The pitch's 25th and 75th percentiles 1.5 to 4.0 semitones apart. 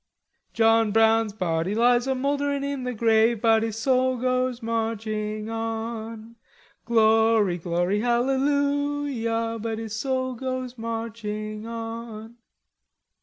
Yes: narrow, 2.4 semitones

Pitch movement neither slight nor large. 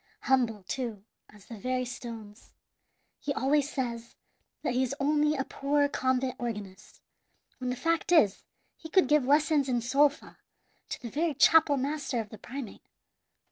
Yes: average, 3.6 semitones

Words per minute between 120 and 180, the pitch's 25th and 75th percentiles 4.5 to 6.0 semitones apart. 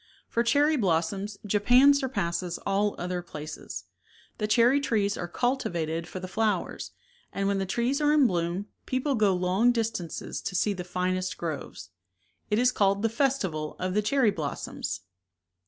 Yes: average, 165 wpm; average, 4.9 semitones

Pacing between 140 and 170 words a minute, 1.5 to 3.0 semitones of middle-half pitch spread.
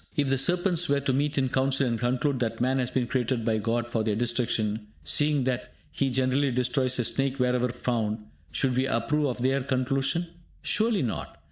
No: average, 195 wpm; narrow, 2.4 semitones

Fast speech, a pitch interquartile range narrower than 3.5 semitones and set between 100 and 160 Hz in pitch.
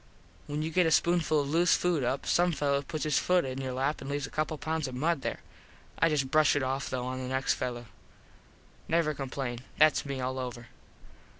Yes: fast, 220 wpm; average, 3.1 semitones; medium, 140 Hz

